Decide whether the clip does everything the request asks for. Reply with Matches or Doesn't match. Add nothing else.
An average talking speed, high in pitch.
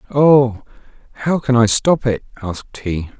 Doesn't match